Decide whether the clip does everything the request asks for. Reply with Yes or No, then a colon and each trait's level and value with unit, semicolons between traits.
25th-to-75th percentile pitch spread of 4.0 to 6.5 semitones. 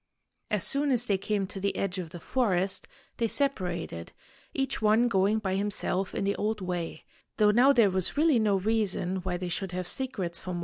No: average, 3.5 semitones